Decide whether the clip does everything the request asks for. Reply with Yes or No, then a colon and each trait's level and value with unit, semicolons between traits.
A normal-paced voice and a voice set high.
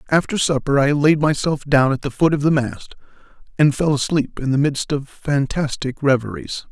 No: average, 190 wpm; medium, 140 Hz